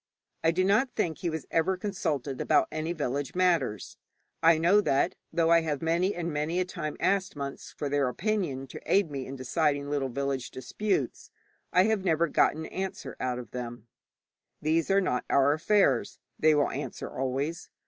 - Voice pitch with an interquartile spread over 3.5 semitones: Yes, average, 4.7 semitones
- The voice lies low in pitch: No, medium, 160 Hz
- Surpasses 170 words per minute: Yes, average, 180 wpm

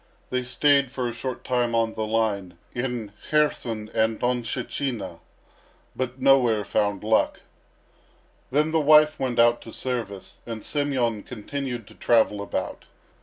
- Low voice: Yes, low, 120 Hz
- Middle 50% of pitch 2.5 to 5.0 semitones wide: Yes, average, 3.2 semitones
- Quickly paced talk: No, slow, 135 wpm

